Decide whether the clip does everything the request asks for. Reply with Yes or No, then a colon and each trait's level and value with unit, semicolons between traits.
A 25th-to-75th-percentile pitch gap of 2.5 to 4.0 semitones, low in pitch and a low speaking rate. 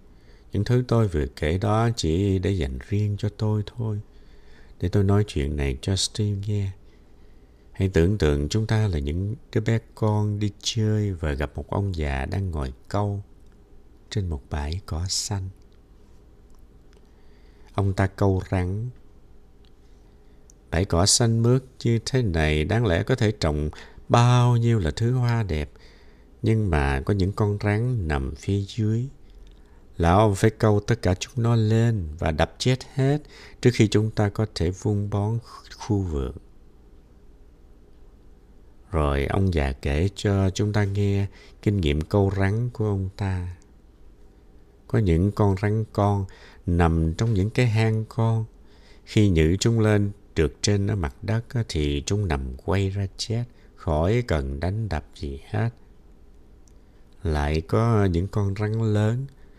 No: average, 5.2 semitones; low, 100 Hz; slow, 155 wpm